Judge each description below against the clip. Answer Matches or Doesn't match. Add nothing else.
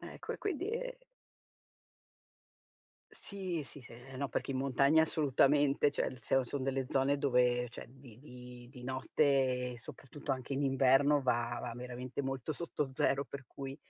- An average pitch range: Doesn't match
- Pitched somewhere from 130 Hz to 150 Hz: Matches